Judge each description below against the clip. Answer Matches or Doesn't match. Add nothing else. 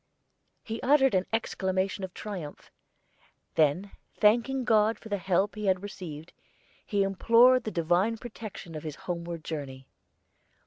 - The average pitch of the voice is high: Matches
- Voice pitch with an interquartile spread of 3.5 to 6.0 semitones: Matches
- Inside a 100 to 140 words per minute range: Matches